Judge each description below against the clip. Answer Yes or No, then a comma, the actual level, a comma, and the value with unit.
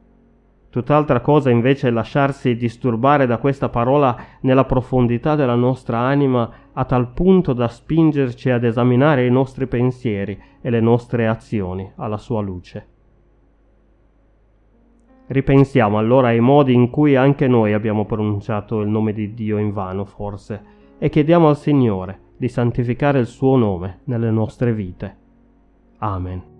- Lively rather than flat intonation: No, average, 4.1 semitones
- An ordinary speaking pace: Yes, average, 140 wpm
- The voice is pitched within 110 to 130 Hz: Yes, low, 120 Hz